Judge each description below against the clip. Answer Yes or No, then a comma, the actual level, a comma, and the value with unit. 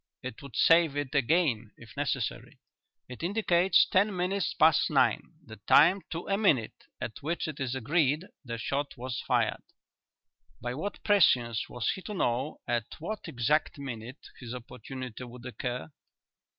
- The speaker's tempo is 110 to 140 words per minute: No, average, 150 wpm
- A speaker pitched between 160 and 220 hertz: No, medium, 140 Hz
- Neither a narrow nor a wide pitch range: No, wide, 5.8 semitones